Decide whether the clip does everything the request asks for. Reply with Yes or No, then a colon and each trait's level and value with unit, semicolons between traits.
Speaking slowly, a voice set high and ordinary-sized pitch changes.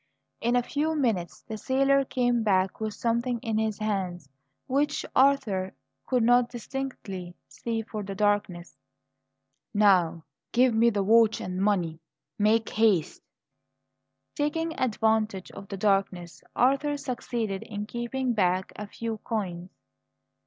Yes: slow, 130 wpm; high, 220 Hz; average, 4.1 semitones